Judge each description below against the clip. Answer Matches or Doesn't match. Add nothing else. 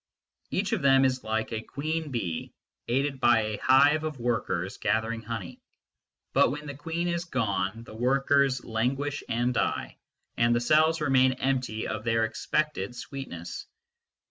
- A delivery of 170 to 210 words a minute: Doesn't match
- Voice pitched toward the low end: Matches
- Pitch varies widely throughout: Doesn't match